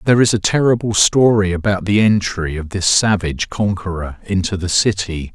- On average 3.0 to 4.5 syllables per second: No, 5.3 syllables/s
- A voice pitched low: Yes, very low, 95 Hz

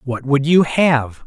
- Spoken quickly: No, average, 190 wpm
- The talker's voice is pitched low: No, medium, 145 Hz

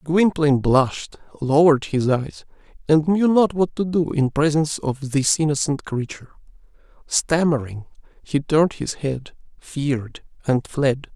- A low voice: No, medium, 150 Hz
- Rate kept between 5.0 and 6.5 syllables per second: No, 4.6 syllables/s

